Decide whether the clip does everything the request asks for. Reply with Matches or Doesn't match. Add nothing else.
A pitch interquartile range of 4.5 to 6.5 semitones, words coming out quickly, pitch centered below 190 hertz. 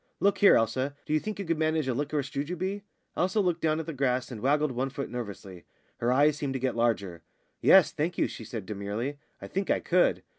Matches